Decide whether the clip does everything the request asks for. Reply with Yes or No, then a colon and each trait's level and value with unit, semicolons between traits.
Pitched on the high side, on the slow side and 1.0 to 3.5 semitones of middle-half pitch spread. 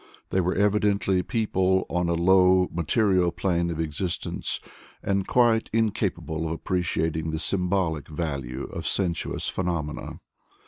No: very low, 90 Hz; slow, 125 wpm; average, 2.9 semitones